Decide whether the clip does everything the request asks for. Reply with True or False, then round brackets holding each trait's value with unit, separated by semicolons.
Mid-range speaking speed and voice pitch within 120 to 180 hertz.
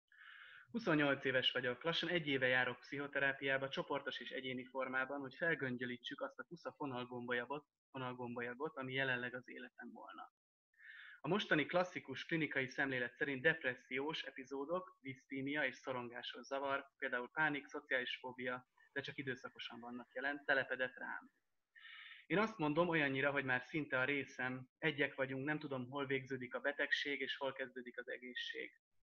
True (140 wpm; 135 Hz)